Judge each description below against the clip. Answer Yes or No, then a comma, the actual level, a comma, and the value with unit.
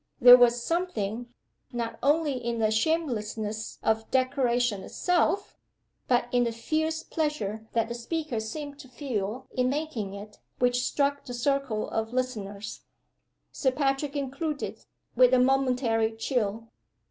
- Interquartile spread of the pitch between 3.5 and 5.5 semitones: Yes, average, 4.0 semitones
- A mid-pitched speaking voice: No, high, 245 Hz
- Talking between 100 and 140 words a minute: Yes, slow, 135 wpm